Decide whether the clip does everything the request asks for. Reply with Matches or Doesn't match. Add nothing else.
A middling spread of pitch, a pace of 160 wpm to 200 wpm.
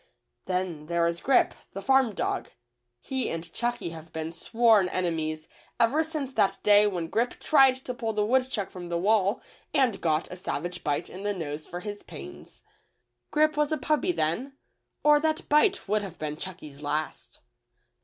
Doesn't match